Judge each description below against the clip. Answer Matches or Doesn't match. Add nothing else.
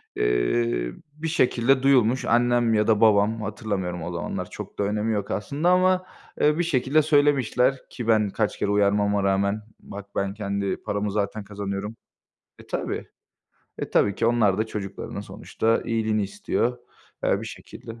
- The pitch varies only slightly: Doesn't match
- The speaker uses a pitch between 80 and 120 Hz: Matches